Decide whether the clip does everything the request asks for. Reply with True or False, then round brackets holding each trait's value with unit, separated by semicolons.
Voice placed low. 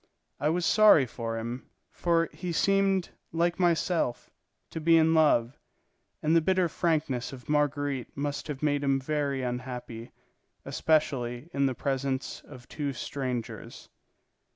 False (145 Hz)